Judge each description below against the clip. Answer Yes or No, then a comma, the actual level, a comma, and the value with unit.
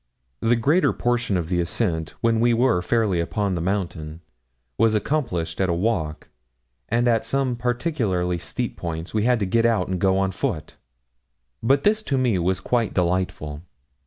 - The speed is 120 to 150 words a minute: No, average, 170 wpm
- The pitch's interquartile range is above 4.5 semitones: Yes, wide, 5.4 semitones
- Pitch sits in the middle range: No, low, 100 Hz